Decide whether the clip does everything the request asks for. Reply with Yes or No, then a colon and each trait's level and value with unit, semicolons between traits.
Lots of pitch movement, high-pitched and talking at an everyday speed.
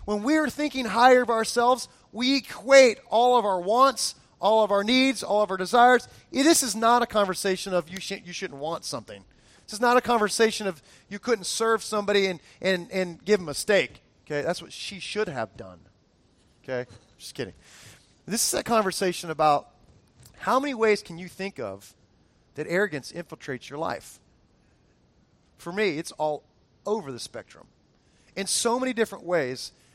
Yes: wide, 5.9 semitones; high, 200 Hz; average, 180 wpm